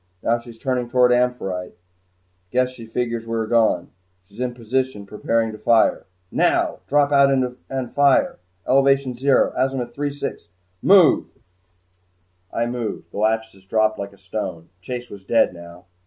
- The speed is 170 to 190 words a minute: No, average, 150 wpm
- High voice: No, low, 120 Hz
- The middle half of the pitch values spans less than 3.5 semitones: Yes, average, 3.0 semitones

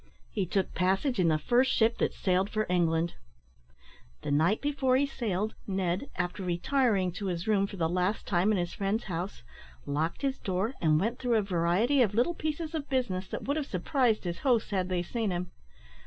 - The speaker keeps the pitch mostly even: No, wide, 5.4 semitones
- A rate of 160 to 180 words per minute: No, average, 200 wpm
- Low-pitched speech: No, high, 195 Hz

